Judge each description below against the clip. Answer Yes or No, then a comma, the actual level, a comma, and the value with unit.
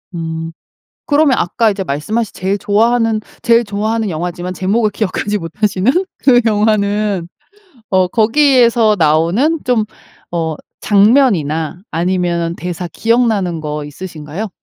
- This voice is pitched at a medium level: No, high, 200 Hz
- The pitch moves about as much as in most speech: Yes, average, 4.8 semitones